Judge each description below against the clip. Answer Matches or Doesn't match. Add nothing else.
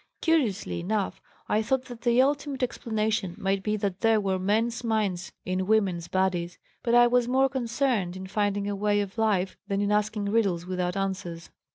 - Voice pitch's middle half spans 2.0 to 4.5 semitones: Matches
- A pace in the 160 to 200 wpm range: Matches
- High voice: Matches